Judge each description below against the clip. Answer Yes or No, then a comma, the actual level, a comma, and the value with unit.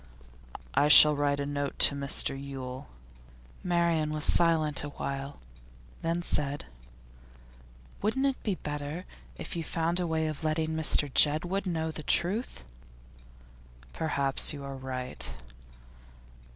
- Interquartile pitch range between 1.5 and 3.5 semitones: Yes, average, 2.9 semitones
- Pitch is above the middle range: No, medium, 150 Hz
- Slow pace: Yes, slow, 125 wpm